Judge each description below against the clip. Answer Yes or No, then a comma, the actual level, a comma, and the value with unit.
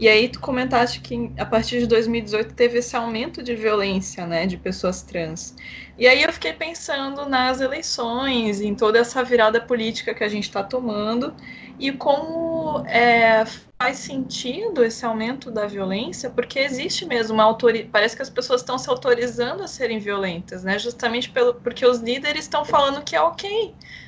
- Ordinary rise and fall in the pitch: Yes, average, 3.1 semitones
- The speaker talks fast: No, average, 175 wpm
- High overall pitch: Yes, high, 240 Hz